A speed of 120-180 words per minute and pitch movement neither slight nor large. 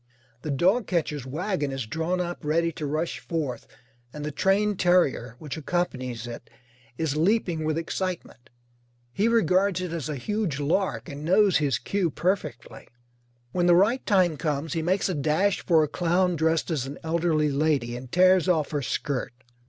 Yes: average, 170 wpm; average, 4.2 semitones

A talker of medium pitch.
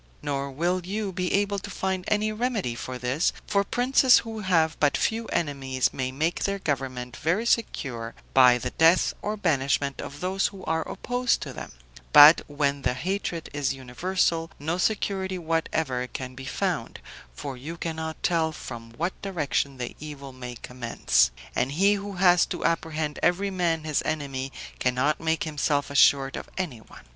Yes: medium, 160 Hz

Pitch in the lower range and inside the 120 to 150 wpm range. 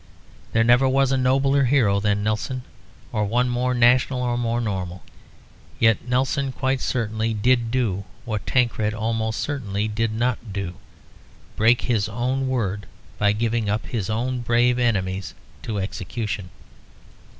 Yes: low, 115 Hz; average, 140 wpm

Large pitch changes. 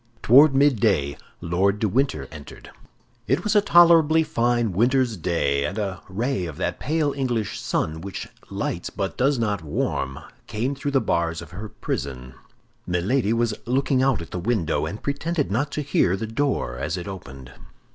Yes: wide, 8.1 semitones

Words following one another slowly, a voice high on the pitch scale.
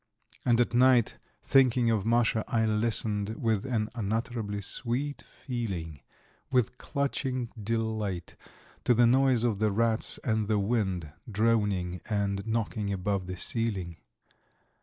No: slow, 125 wpm; low, 110 Hz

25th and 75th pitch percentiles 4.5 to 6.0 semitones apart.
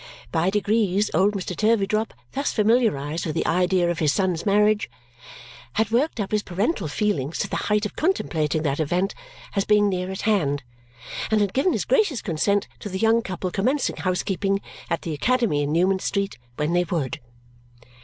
No: average, 4.0 semitones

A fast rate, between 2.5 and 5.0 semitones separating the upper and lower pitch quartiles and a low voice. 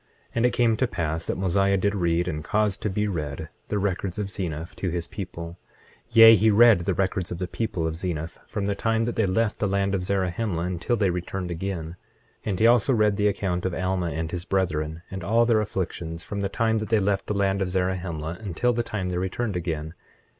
Yes: fast, 225 wpm; average, 3.4 semitones; very low, 95 Hz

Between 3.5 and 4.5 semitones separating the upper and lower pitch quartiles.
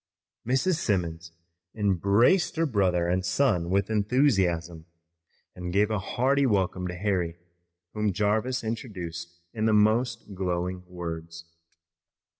Yes: average, 4.0 semitones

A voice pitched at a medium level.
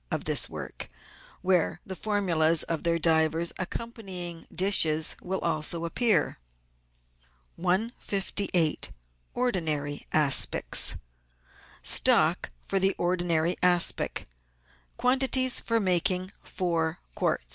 Yes: medium, 175 Hz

